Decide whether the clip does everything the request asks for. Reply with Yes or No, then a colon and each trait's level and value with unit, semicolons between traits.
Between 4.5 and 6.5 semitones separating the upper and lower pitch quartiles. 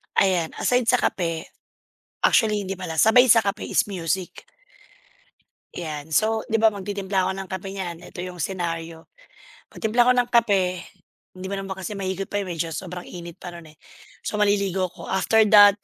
No: average, 3.0 semitones